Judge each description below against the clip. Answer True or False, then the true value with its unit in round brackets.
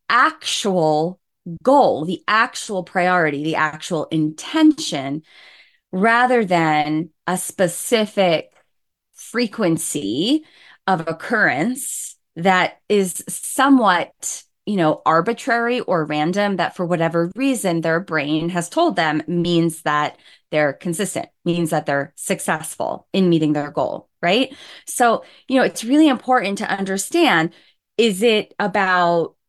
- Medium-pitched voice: True (180 Hz)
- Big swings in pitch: True (6.2 semitones)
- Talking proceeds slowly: True (115 wpm)